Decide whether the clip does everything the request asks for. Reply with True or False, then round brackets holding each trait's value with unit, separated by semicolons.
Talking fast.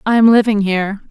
False (165 wpm)